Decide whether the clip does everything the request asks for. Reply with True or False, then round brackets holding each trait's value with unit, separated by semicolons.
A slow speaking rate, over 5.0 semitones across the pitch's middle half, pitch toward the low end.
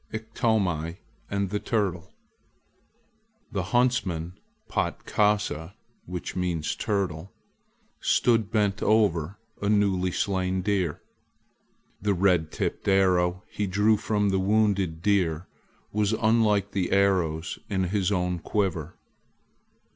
False (100 wpm; 2.7 semitones; 100 Hz)